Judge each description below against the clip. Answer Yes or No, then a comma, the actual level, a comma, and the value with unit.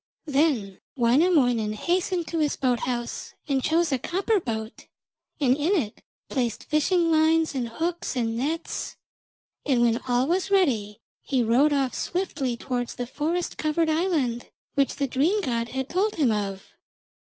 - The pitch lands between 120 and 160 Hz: No, very high, 275 Hz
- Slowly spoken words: No, average, 155 wpm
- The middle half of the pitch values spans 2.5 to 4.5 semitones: No, wide, 5.5 semitones